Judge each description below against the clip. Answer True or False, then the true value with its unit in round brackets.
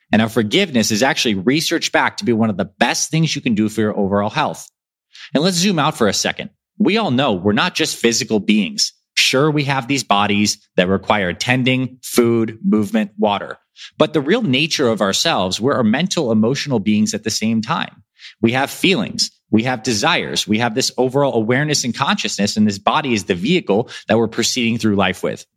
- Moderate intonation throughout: False (5.8 semitones)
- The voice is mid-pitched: False (115 Hz)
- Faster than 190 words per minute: True (205 wpm)